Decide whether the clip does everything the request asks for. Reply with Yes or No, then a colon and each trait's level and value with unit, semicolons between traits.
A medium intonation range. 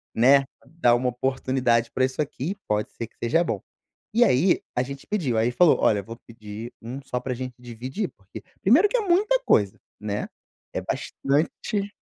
No: wide, 6.3 semitones